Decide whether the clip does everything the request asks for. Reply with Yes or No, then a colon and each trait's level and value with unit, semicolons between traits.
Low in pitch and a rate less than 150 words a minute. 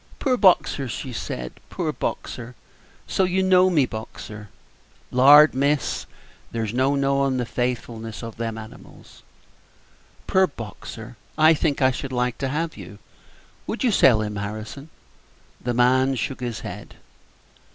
Yes: low, 130 Hz; average, 140 wpm